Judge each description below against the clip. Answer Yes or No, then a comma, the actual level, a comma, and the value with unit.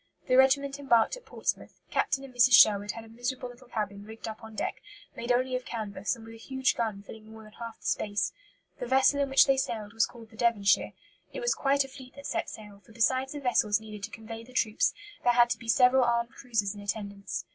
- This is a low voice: No, high, 235 Hz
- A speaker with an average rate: No, fast, 235 wpm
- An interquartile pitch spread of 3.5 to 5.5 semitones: No, average, 3.1 semitones